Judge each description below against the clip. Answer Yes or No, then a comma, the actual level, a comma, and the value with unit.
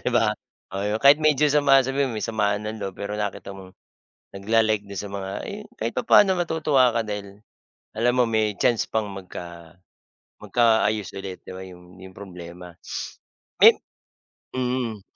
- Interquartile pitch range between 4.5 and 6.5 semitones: No, average, 4.0 semitones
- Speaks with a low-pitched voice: Yes, low, 105 Hz